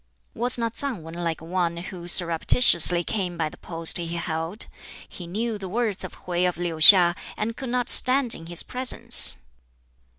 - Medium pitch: Yes, medium, 180 Hz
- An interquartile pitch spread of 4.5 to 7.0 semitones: Yes, average, 5.2 semitones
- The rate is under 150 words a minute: No, average, 175 wpm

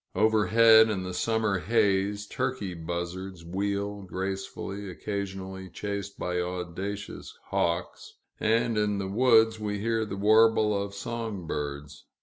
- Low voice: Yes, low, 100 Hz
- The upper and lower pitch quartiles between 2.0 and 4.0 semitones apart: Yes, average, 2.7 semitones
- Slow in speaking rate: Yes, slow, 125 wpm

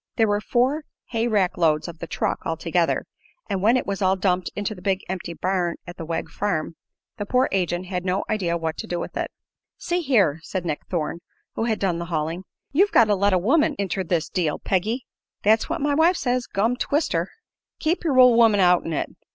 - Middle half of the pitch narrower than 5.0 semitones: No, wide, 5.4 semitones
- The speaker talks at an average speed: No, fast, 215 wpm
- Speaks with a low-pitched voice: No, high, 195 Hz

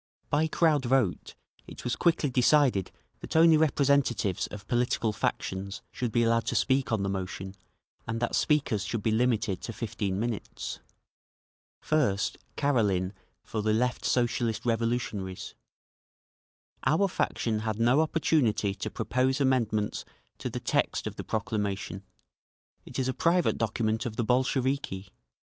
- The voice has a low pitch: Yes, low, 115 Hz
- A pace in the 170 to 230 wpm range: No, average, 140 wpm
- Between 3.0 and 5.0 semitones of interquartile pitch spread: Yes, average, 4.1 semitones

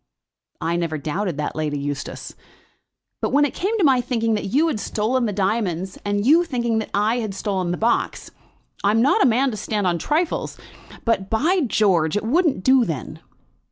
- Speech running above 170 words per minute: Yes, average, 190 wpm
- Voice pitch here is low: No, high, 215 Hz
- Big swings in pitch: Yes, wide, 5.7 semitones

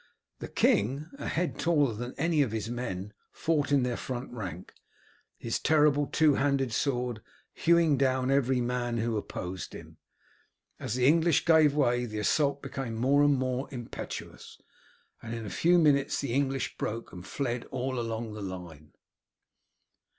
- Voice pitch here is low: Yes, low, 130 Hz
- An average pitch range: Yes, average, 3.8 semitones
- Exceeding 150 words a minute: Yes, average, 160 wpm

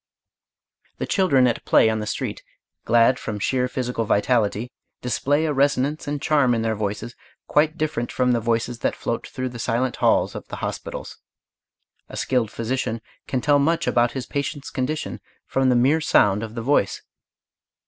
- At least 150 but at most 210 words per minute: Yes, average, 170 wpm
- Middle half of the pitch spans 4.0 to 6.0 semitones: No, average, 3.5 semitones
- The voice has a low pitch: Yes, low, 125 Hz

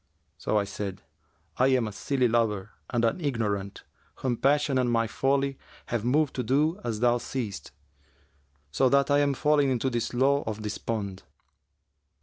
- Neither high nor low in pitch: No, low, 120 Hz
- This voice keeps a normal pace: Yes, average, 160 wpm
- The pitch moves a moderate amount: Yes, average, 4.1 semitones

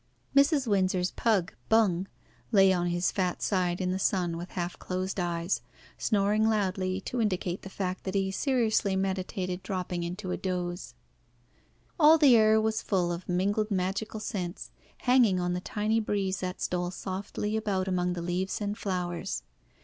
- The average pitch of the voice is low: No, high, 190 Hz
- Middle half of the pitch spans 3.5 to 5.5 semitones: No, average, 2.7 semitones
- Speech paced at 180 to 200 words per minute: No, average, 160 wpm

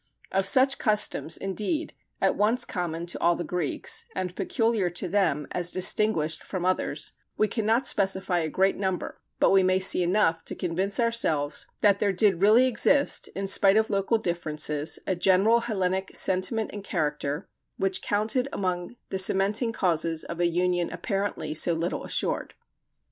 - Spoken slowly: No, average, 160 wpm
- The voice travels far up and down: No, average, 3.3 semitones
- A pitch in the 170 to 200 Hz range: Yes, high, 190 Hz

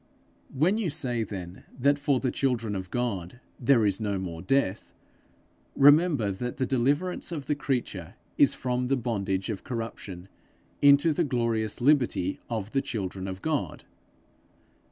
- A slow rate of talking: No, average, 150 wpm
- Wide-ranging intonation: Yes, wide, 5.9 semitones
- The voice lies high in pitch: No, low, 120 Hz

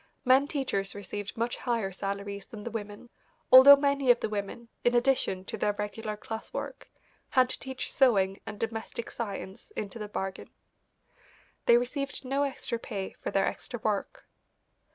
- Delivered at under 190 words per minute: Yes, average, 160 wpm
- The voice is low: No, high, 225 Hz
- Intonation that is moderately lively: Yes, average, 4.1 semitones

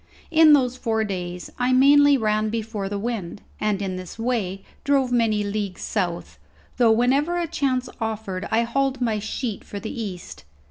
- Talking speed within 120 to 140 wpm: No, average, 170 wpm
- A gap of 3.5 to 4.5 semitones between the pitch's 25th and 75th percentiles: Yes, average, 4.1 semitones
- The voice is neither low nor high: No, high, 225 Hz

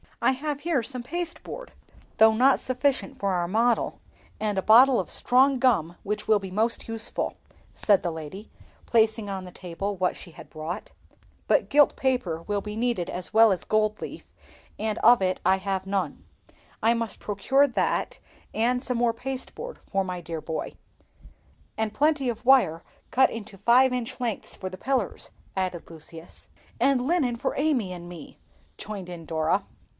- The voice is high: Yes, high, 220 Hz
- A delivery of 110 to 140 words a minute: No, average, 170 wpm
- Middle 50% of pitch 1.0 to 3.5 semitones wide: No, average, 5.3 semitones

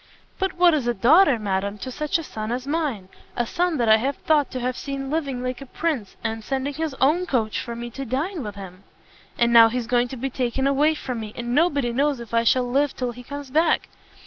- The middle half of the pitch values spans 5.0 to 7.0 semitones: No, average, 3.7 semitones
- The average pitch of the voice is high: Yes, very high, 255 Hz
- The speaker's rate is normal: No, fast, 235 wpm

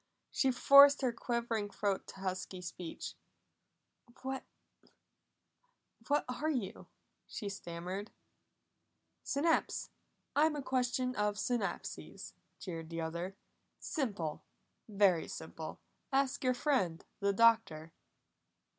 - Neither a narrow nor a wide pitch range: No, wide, 5.9 semitones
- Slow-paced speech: Yes, slow, 100 wpm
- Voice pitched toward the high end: Yes, high, 215 Hz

